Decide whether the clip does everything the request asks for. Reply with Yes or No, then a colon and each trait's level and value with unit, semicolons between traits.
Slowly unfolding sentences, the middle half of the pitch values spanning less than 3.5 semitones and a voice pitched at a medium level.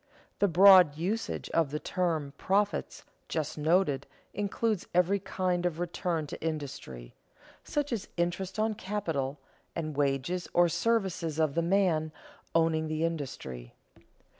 No: slow, 130 wpm; average, 3.9 semitones; medium, 170 Hz